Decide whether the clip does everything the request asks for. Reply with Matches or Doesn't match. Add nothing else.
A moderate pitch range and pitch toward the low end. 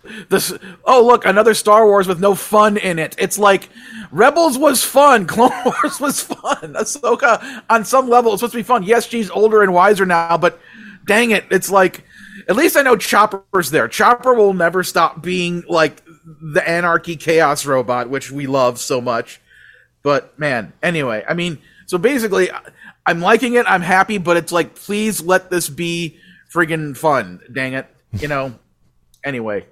Doesn't match